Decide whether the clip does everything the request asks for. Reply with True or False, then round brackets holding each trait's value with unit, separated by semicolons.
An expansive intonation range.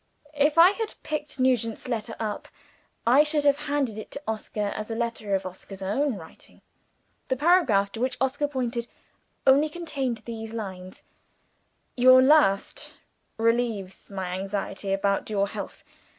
True (5.8 semitones)